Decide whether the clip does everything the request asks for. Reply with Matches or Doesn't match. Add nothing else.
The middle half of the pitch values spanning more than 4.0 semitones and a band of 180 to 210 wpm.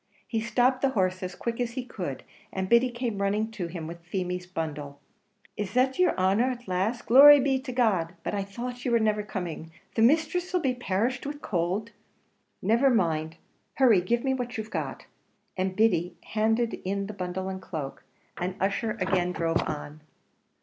Matches